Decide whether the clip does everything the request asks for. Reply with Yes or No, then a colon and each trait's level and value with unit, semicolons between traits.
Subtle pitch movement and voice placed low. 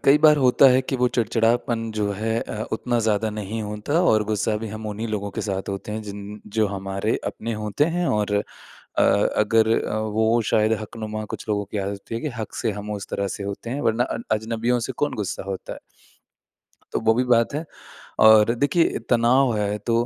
Yes: narrow, 2.2 semitones; low, 110 Hz